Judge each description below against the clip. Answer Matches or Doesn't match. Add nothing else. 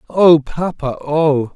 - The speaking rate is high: Doesn't match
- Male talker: Matches